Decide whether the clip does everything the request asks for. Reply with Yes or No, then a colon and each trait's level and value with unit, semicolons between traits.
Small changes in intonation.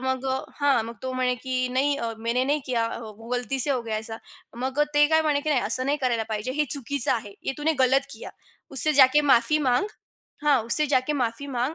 No: average, 3.4 semitones